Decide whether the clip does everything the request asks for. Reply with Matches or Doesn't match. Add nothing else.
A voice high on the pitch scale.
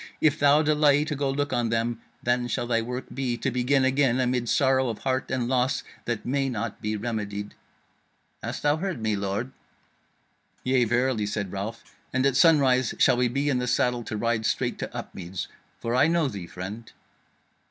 Doesn't match